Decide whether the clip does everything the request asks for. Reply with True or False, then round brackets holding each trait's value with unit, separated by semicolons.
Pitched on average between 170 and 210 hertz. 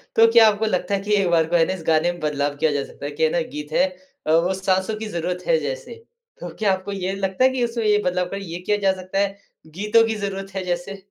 True (190 Hz)